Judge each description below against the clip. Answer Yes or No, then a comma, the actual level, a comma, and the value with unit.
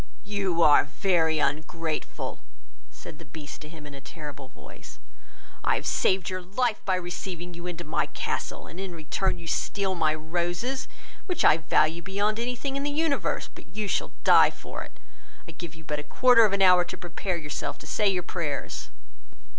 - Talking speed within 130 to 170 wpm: No, average, 190 wpm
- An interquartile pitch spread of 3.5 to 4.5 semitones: Yes, average, 4.0 semitones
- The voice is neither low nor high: Yes, medium, 175 Hz